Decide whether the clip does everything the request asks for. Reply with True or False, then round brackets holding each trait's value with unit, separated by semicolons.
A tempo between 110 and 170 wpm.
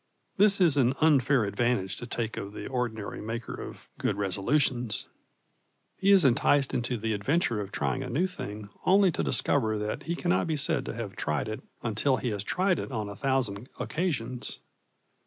False (180 wpm)